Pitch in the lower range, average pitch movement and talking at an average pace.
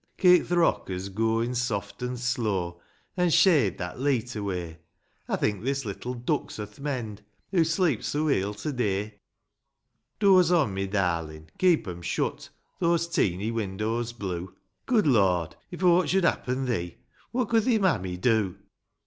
No: low, 115 Hz; wide, 8.5 semitones; average, 155 wpm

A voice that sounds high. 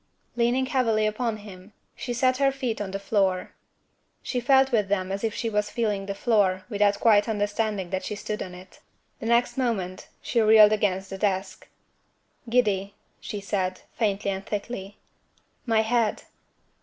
Yes: high, 210 Hz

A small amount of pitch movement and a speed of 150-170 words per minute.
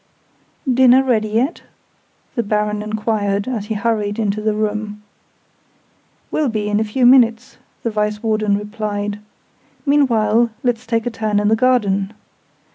No: narrow, 2.1 semitones; average, 140 wpm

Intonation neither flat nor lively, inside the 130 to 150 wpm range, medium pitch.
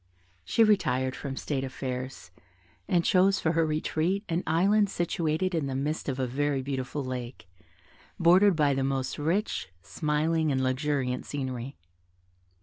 Yes: average, 4.2 semitones; average, 145 wpm; medium, 145 Hz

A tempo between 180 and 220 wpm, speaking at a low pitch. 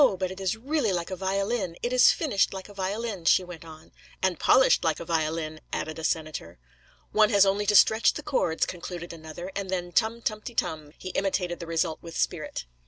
No: average, 200 wpm; medium, 185 Hz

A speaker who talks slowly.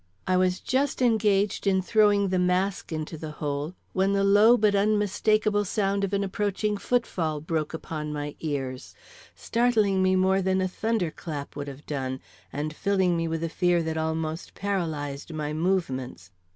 No: average, 170 wpm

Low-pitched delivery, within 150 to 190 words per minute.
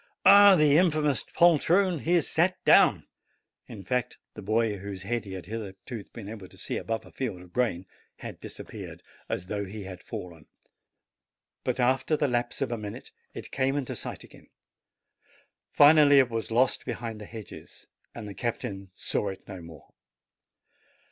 Yes: low, 115 Hz; average, 170 wpm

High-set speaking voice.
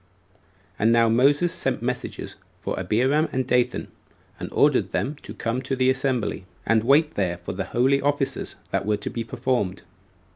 No: low, 125 Hz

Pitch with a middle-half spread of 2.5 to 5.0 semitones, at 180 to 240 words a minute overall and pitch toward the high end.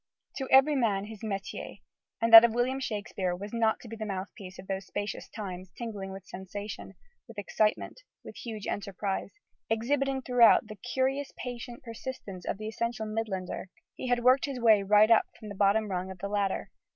Yes: average, 3.3 semitones; average, 185 wpm; high, 215 Hz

